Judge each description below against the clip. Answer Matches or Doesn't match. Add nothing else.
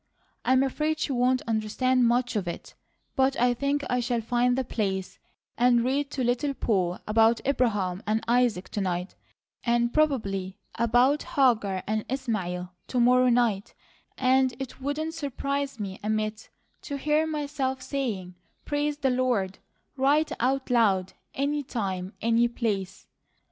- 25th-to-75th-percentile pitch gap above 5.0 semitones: Doesn't match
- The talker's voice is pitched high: Matches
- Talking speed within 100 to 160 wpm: Matches